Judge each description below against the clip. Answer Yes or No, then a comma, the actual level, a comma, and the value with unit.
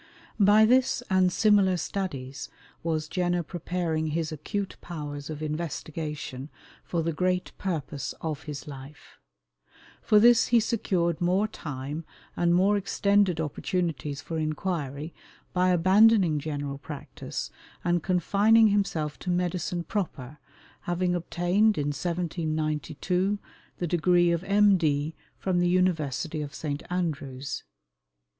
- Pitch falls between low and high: Yes, medium, 170 Hz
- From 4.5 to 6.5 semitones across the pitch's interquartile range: No, average, 3.6 semitones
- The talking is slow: Yes, slow, 120 wpm